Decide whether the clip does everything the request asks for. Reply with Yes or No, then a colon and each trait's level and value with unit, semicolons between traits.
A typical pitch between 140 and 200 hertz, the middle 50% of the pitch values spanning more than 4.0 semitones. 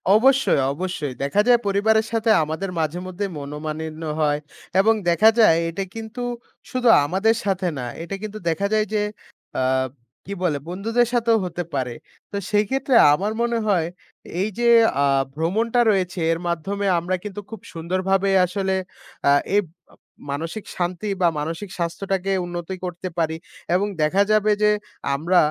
Yes: high, 190 Hz; average, 4.5 semitones